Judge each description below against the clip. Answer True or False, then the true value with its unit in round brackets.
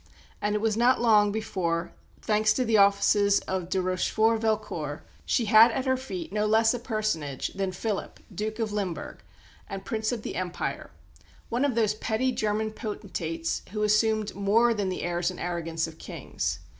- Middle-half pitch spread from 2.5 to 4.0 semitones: True (3.1 semitones)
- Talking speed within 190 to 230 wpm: False (175 wpm)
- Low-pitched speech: False (210 Hz)